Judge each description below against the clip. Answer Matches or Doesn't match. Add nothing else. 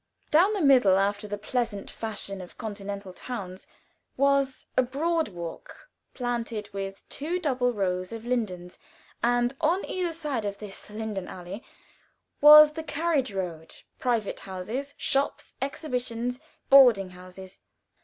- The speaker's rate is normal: Doesn't match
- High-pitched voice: Matches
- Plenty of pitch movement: Matches